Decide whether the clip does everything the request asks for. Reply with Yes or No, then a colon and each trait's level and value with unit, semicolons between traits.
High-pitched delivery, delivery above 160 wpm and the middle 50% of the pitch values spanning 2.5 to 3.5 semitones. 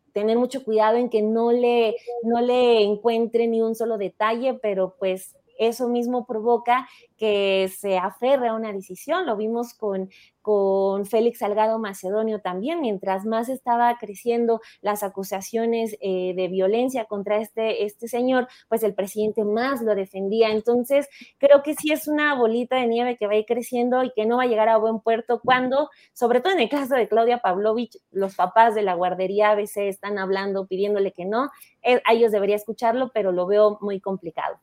Yes: high, 225 Hz; average, 185 wpm; average, 2.9 semitones